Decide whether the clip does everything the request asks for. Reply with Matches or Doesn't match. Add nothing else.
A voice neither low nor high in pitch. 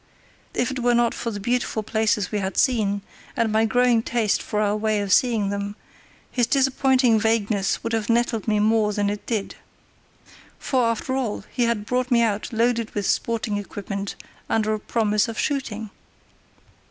Doesn't match